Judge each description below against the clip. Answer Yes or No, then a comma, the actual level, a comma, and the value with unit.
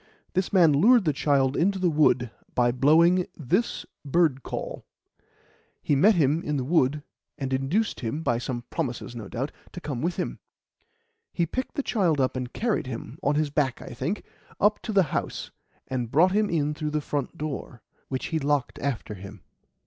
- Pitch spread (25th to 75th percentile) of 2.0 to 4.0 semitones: No, average, 4.9 semitones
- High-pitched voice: No, medium, 150 Hz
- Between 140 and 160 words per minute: No, average, 185 wpm